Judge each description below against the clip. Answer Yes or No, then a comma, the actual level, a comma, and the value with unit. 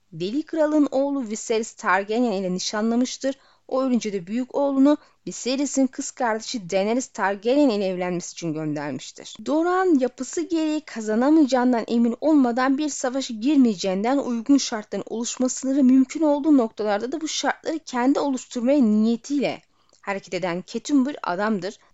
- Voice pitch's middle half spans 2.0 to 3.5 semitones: No, average, 4.4 semitones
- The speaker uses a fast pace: No, average, 130 wpm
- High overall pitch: Yes, very high, 250 Hz